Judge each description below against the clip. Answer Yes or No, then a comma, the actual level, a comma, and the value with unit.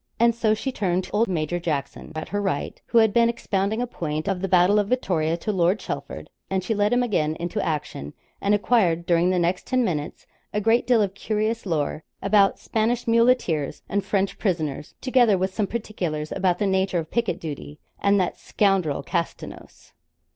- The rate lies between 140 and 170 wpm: No, average, 190 wpm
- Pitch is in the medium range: No, high, 195 Hz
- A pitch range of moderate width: Yes, average, 4.3 semitones